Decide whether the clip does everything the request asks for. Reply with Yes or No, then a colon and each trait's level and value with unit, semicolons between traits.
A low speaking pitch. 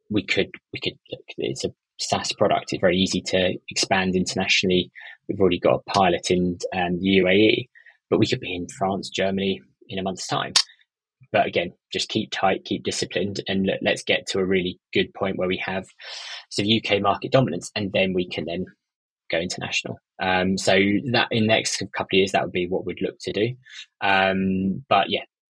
Yes: very low, 95 Hz